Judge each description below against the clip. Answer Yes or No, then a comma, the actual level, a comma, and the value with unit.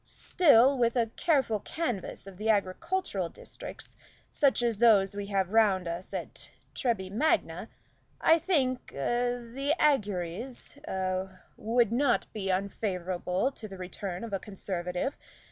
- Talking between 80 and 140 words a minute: Yes, slow, 135 wpm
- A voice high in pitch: Yes, high, 215 Hz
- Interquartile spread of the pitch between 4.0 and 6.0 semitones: Yes, average, 4.9 semitones